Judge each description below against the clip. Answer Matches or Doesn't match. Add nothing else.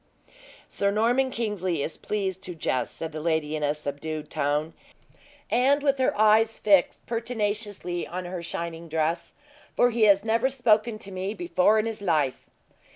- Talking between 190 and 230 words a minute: Doesn't match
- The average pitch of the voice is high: Matches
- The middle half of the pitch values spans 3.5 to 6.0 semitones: Matches